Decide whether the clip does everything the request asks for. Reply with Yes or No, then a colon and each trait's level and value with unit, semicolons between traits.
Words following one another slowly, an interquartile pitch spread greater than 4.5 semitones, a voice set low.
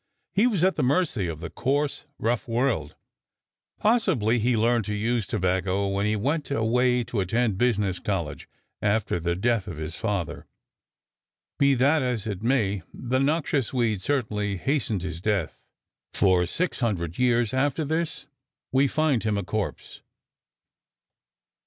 No: average, 145 wpm; average, 5.3 semitones; low, 115 Hz